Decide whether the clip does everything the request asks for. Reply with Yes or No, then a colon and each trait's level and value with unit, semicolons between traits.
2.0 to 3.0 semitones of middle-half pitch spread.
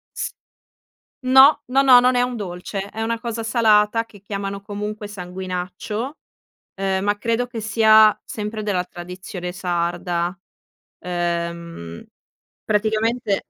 No: average, 3.9 semitones